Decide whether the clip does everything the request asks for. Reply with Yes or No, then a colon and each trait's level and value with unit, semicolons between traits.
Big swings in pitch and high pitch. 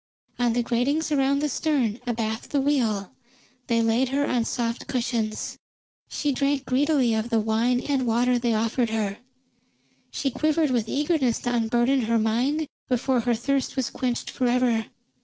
No: average, 3.2 semitones; high, 245 Hz